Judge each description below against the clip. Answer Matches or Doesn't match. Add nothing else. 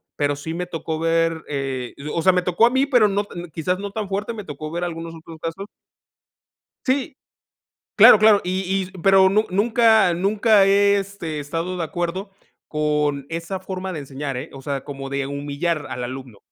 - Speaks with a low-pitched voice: Doesn't match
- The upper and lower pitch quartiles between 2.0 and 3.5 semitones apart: Doesn't match